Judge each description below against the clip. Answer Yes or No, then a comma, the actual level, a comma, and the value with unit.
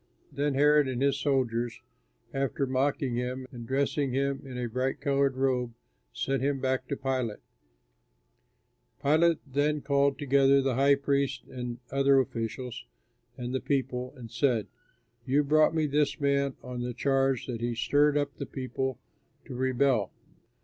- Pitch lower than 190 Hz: Yes, low, 135 Hz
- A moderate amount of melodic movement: No, narrow, 1.9 semitones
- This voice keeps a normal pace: Yes, average, 150 wpm